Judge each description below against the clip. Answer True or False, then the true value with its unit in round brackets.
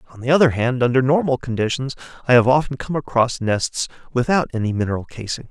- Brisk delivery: False (185 wpm)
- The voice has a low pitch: True (125 Hz)